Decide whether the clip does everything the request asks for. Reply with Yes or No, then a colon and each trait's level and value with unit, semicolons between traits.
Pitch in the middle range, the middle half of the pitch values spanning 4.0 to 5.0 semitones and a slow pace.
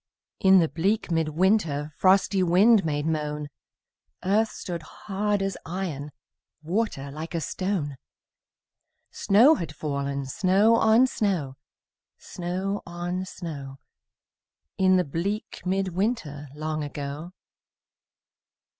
Yes: medium, 175 Hz; average, 4.6 semitones; slow, 110 wpm